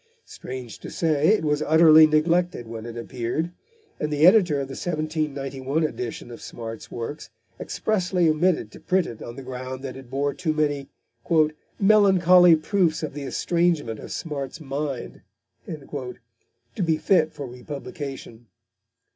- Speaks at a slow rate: No, average, 145 wpm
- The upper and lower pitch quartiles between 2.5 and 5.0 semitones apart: Yes, average, 4.2 semitones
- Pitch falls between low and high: Yes, medium, 150 Hz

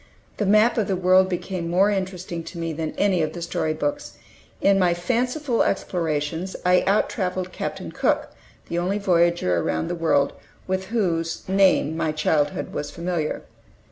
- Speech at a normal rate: Yes, average, 165 wpm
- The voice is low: No, medium, 180 Hz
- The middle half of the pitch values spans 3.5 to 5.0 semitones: No, average, 2.8 semitones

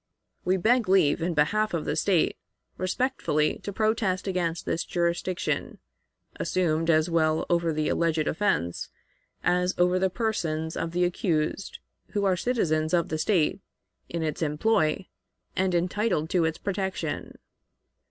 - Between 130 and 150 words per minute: Yes, average, 140 wpm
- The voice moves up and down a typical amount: Yes, average, 3.2 semitones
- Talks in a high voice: No, medium, 175 Hz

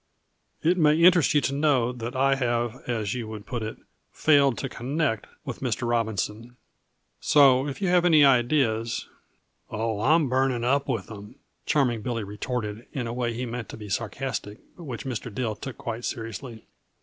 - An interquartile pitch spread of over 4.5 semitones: No, average, 3.4 semitones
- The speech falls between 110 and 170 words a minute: No, average, 180 wpm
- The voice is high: No, low, 120 Hz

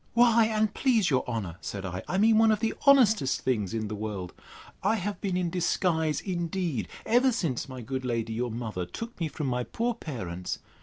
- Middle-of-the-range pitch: Yes, medium, 160 Hz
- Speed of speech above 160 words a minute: Yes, average, 200 wpm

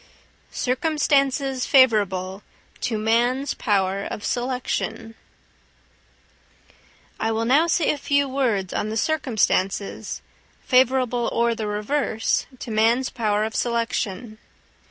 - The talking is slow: Yes, slow, 105 wpm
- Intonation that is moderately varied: Yes, average, 3.6 semitones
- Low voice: No, high, 235 Hz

